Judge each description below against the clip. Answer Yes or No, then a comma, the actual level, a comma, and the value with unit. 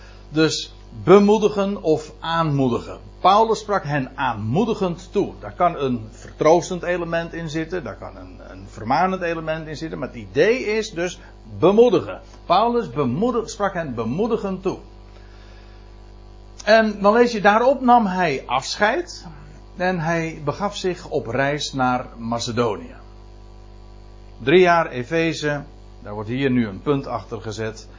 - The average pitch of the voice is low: No, medium, 145 Hz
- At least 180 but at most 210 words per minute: No, slow, 135 wpm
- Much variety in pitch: Yes, wide, 8.9 semitones